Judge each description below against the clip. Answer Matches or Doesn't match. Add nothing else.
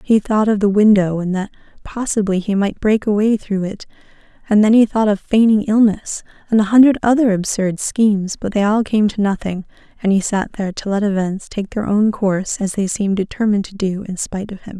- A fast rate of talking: Matches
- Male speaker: Doesn't match